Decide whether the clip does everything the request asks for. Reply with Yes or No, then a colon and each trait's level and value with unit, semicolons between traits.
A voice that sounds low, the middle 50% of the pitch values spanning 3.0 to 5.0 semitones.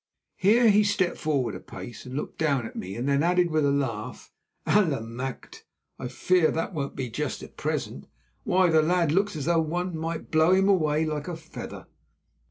No: medium, 160 Hz; average, 4.4 semitones